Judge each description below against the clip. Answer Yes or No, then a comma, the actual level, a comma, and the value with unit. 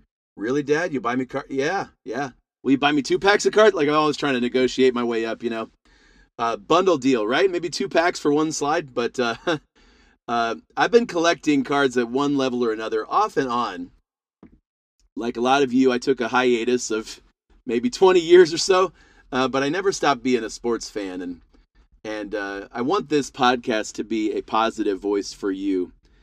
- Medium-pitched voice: No, low, 130 Hz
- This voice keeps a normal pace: No, fast, 210 wpm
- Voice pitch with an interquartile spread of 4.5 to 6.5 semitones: Yes, average, 4.9 semitones